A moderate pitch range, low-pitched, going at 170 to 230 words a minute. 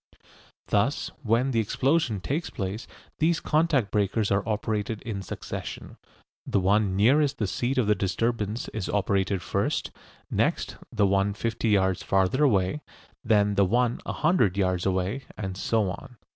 No: average, 3.8 semitones; low, 105 Hz; average, 150 wpm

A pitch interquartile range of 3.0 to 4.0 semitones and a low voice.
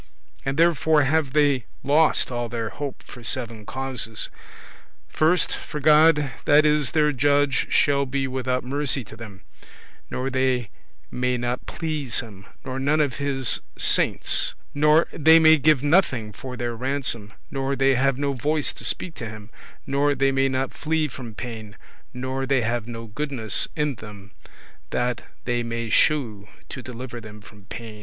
Yes: average, 3.6 semitones; low, 130 Hz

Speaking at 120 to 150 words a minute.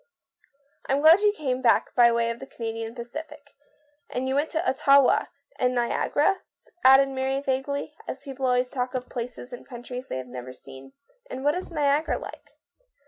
No: average, 180 wpm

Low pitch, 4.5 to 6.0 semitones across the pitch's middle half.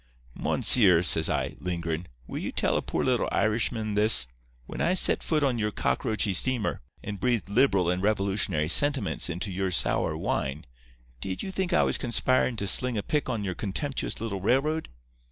Yes: low, 105 Hz; wide, 5.5 semitones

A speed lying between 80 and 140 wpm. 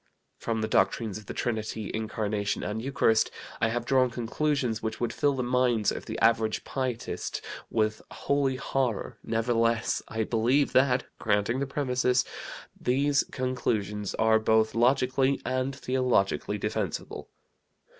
Yes: slow, 135 wpm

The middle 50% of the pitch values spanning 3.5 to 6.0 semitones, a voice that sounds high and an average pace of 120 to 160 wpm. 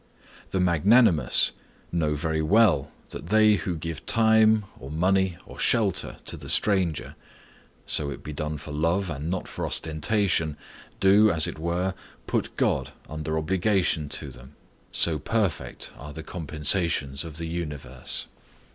No: average, 4.1 semitones; very low, 85 Hz; average, 140 wpm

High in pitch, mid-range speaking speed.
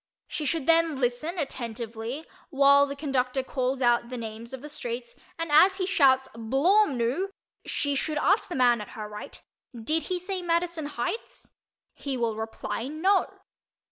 Yes: very high, 275 Hz; average, 160 wpm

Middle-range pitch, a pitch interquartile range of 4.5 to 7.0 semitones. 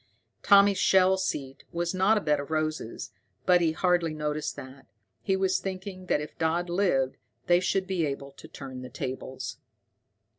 Yes: medium, 170 Hz; average, 4.8 semitones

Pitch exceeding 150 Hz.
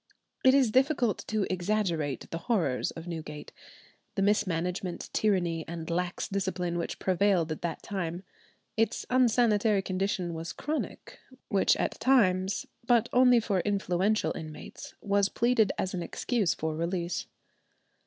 Yes: high, 190 Hz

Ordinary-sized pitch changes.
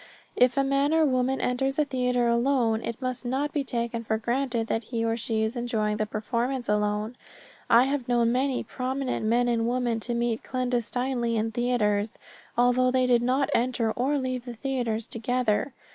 No: narrow, 1.9 semitones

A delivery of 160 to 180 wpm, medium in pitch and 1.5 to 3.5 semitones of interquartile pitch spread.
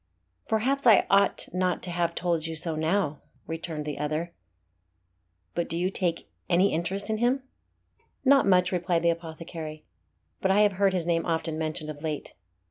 Yes: average, 170 wpm; medium, 170 Hz; average, 3.1 semitones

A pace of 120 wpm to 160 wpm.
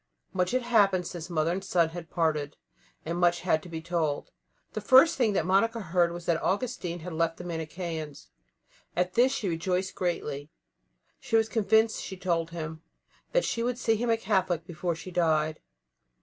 No: average, 180 wpm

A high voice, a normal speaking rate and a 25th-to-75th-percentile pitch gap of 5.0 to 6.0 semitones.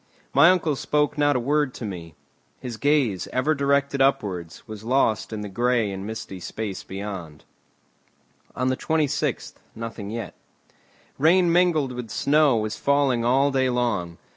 No: low, 125 Hz; average, 150 wpm; average, 5.3 semitones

